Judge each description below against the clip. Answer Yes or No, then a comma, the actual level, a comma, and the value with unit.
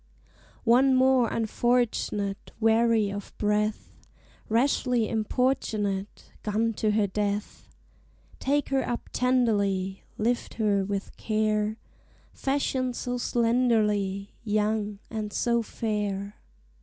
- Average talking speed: No, slow, 95 wpm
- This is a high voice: Yes, high, 220 Hz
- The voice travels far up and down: No, average, 2.7 semitones